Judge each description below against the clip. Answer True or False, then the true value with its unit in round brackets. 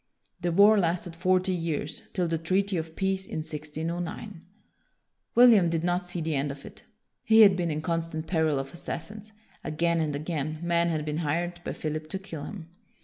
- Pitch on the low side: False (170 Hz)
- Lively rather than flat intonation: False (2.8 semitones)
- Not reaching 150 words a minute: False (185 wpm)